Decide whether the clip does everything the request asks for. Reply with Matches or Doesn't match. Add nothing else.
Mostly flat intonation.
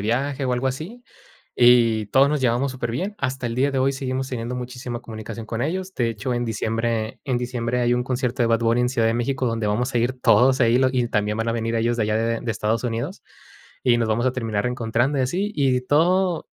Matches